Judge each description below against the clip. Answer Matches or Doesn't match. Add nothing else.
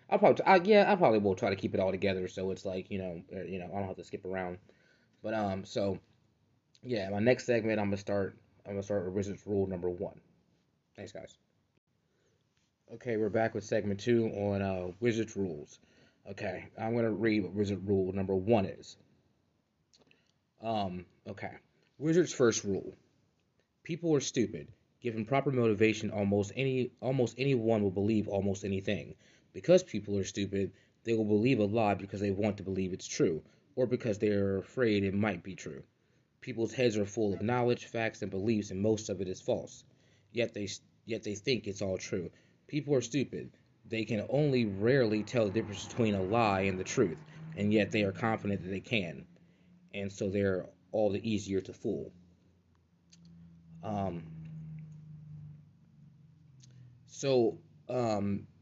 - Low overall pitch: Matches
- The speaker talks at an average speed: Matches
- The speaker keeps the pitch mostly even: Doesn't match